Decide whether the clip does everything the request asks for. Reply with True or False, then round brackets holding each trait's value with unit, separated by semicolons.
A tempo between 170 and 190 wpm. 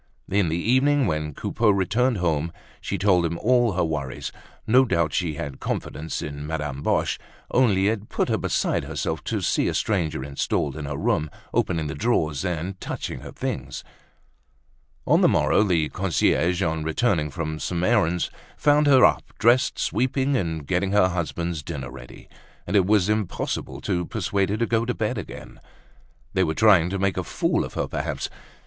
True (180 wpm)